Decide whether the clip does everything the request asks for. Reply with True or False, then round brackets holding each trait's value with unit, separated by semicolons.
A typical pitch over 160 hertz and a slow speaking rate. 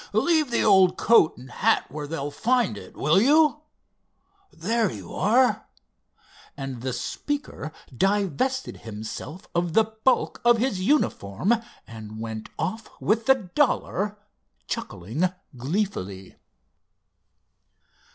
True (190 Hz; 110 wpm)